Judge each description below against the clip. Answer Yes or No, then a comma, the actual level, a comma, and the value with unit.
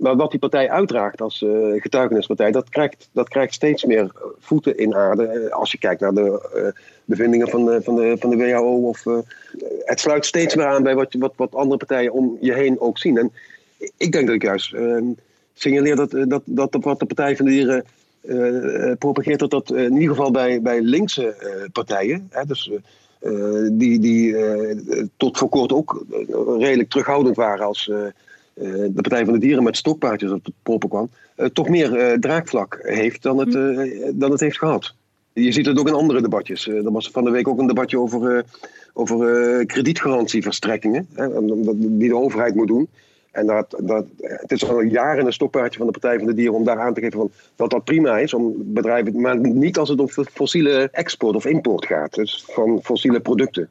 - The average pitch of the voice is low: Yes, low, 125 Hz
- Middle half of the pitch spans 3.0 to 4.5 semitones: Yes, average, 3.6 semitones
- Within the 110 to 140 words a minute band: No, fast, 200 wpm